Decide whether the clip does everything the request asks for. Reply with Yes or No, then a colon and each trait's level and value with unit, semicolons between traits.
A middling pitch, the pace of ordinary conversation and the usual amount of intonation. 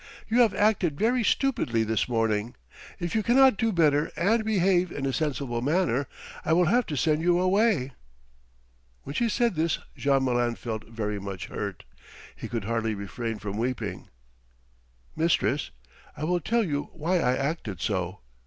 No: medium, 150 Hz; average, 160 wpm; wide, 8.1 semitones